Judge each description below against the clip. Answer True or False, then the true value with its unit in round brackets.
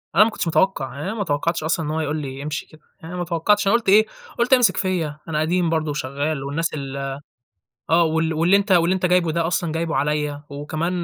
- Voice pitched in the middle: True (160 Hz)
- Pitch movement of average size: True (3.3 semitones)